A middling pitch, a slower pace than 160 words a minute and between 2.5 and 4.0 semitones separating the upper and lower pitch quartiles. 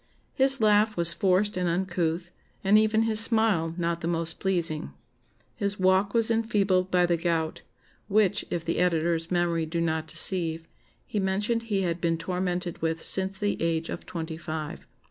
No: medium, 180 Hz; average, 165 wpm; average, 3.4 semitones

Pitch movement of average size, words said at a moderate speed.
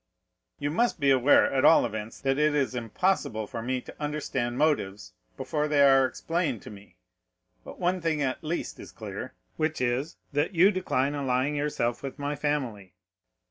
Yes: average, 3.6 semitones; average, 175 wpm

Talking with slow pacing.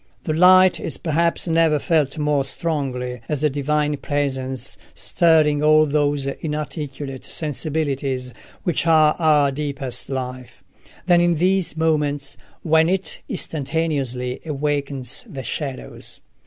Yes: slow, 115 wpm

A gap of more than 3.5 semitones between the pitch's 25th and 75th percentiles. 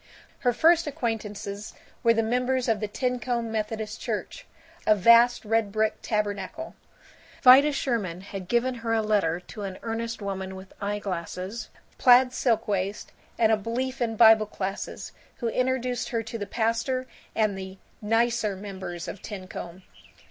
No: average, 3.1 semitones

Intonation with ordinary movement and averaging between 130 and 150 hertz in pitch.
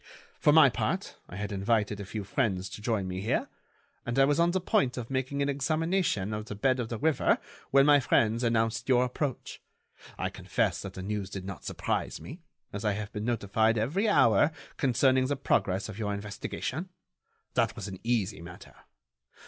No: average, 4.8 semitones; low, 115 Hz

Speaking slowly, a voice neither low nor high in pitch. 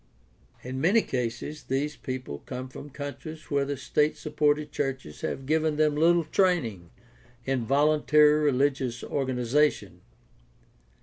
Yes: slow, 120 wpm; medium, 145 Hz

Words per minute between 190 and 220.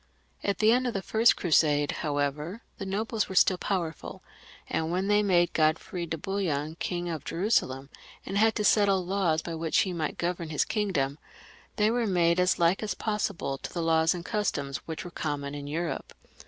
Yes: average, 195 wpm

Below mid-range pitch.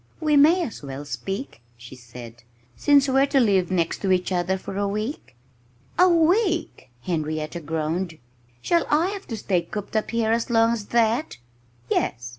No: high, 205 Hz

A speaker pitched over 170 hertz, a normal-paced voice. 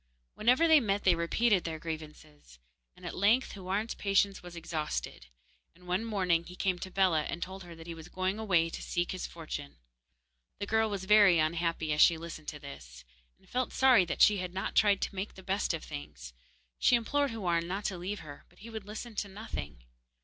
No: medium, 185 Hz; fast, 210 wpm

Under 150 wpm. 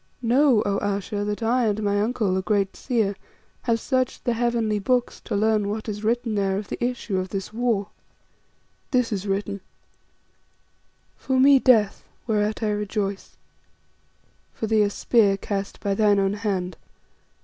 No: average, 160 wpm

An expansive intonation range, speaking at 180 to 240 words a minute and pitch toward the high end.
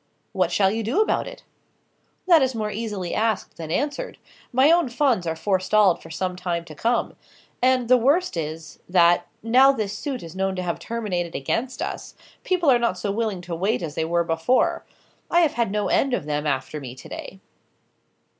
Yes: wide, 6.6 semitones; average, 195 wpm; high, 205 Hz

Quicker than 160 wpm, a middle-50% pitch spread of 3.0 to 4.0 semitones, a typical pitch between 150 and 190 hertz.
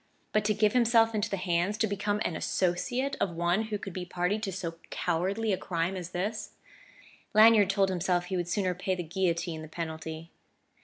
Yes: average, 195 wpm; average, 3.3 semitones; medium, 185 Hz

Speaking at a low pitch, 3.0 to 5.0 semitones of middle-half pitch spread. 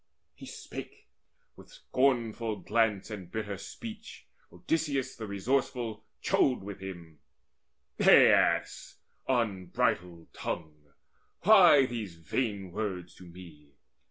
No: low, 105 Hz; wide, 5.5 semitones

